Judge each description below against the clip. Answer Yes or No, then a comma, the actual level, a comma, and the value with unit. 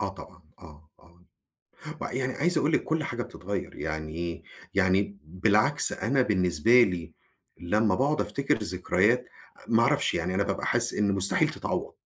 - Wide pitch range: Yes, wide, 5.7 semitones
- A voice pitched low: Yes, low, 100 Hz